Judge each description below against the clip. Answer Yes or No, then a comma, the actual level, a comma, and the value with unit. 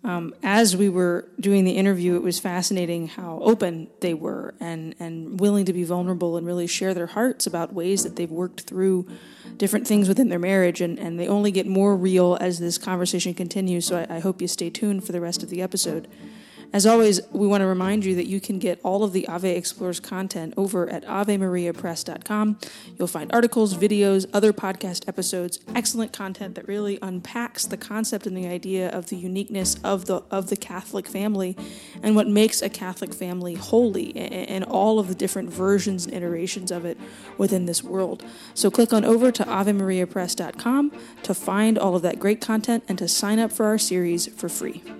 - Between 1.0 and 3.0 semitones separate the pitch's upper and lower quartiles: Yes, narrow, 2.4 semitones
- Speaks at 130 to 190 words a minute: No, average, 200 wpm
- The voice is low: No, high, 190 Hz